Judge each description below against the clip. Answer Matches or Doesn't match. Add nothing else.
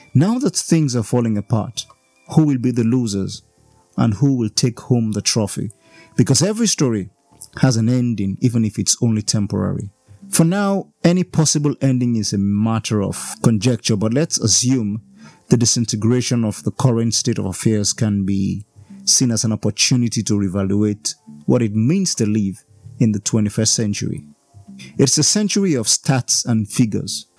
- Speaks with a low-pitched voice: Matches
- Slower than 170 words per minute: Matches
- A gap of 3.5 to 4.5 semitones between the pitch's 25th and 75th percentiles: Matches